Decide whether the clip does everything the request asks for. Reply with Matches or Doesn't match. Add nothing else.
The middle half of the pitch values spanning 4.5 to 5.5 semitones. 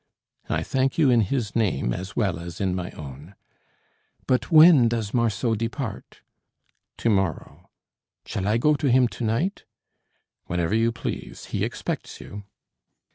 Matches